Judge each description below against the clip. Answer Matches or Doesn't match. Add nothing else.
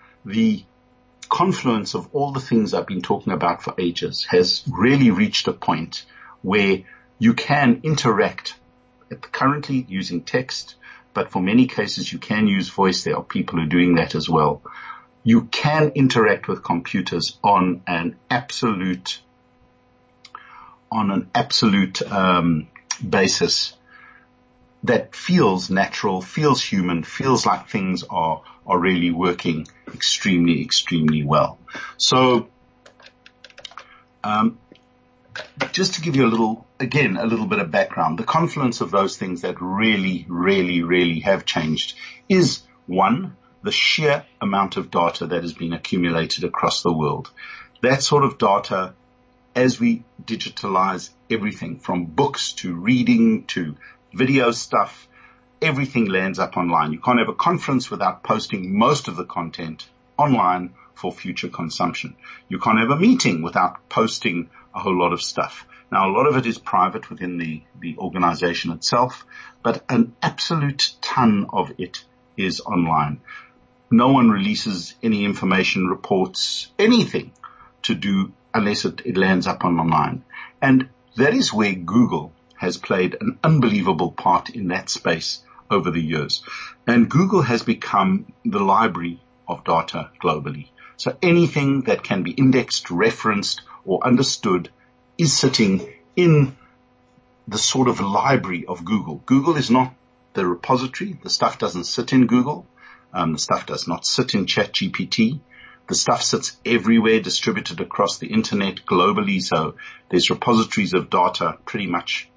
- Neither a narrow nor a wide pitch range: Doesn't match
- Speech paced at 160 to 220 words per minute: Doesn't match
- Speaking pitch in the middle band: Doesn't match